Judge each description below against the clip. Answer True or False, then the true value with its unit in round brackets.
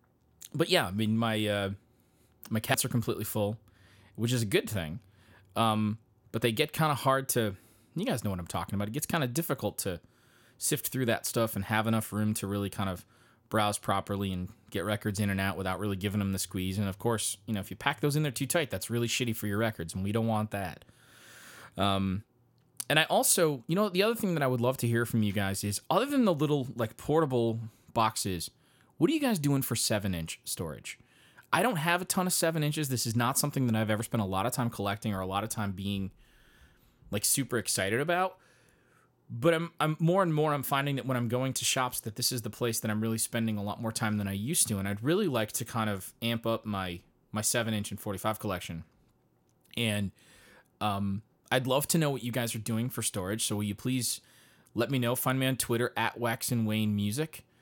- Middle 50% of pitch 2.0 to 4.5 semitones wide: True (3.9 semitones)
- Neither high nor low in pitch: False (115 Hz)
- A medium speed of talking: False (240 wpm)